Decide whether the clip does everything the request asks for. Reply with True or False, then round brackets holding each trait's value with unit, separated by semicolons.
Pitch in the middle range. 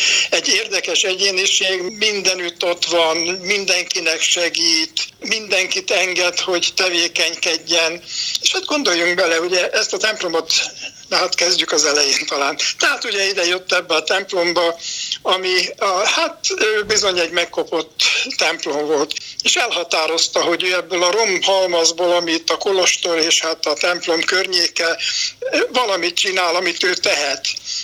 True (180 Hz)